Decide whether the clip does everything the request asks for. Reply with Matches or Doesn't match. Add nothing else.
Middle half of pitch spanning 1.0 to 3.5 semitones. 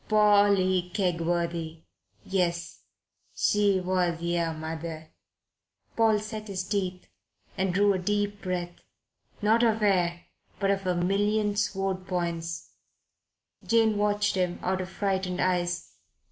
Matches